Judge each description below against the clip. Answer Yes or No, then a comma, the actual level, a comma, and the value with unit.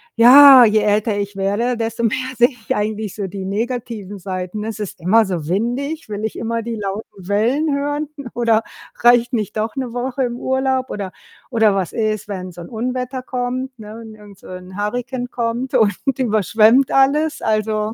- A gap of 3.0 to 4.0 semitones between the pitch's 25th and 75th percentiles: Yes, average, 3.4 semitones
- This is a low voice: No, high, 225 Hz